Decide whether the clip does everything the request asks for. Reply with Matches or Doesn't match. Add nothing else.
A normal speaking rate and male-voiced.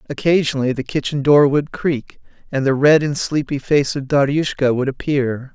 Matches